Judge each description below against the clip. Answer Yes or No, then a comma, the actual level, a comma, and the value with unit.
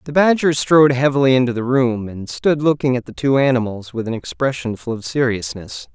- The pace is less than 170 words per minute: No, average, 200 wpm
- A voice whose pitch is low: Yes, low, 125 Hz